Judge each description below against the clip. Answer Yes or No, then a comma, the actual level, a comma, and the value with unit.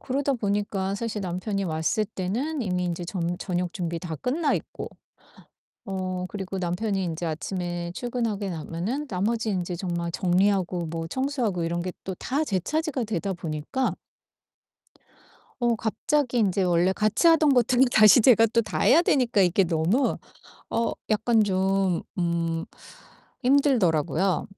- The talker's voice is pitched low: No, high, 195 Hz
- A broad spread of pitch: No, average, 5.0 semitones